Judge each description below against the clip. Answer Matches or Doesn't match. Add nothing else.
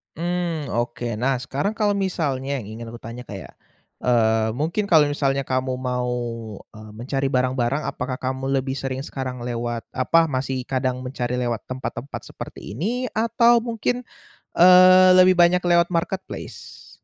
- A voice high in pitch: Doesn't match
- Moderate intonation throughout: Doesn't match